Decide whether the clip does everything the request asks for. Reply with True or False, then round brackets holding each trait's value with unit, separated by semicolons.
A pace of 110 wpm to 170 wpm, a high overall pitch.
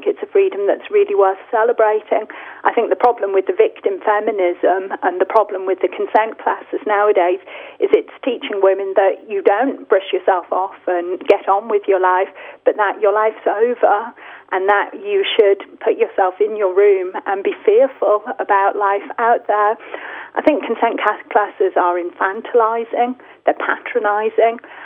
True (165 wpm; 225 Hz)